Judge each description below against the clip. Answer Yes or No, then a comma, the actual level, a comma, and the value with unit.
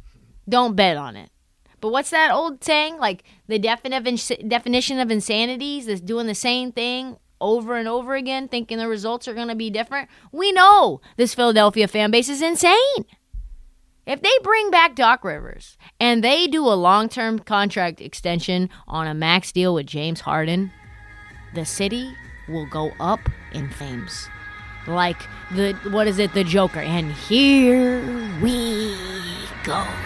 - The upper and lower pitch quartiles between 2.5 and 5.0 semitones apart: No, wide, 5.4 semitones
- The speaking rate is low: No, average, 155 wpm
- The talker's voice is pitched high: Yes, high, 225 Hz